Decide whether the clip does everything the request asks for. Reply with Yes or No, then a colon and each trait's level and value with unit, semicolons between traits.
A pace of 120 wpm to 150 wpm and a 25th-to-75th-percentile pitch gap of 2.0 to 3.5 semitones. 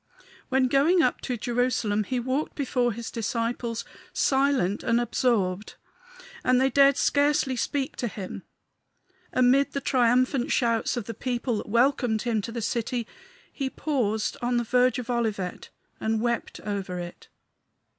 Yes: average, 145 wpm; average, 2.7 semitones